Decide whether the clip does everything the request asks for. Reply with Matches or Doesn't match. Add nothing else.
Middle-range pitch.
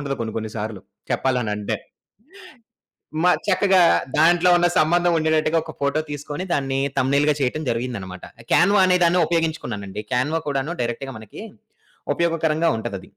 Matches